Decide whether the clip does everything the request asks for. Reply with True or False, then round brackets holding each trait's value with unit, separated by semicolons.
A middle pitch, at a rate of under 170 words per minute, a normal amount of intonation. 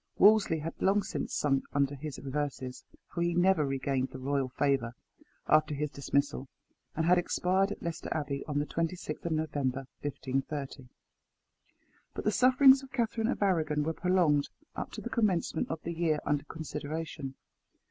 True (155 Hz; 160 wpm; 4.1 semitones)